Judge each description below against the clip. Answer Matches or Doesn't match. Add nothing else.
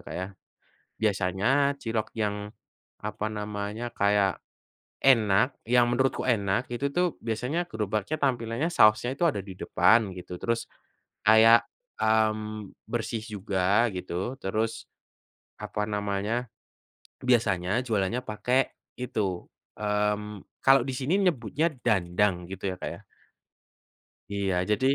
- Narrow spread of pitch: Doesn't match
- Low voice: Matches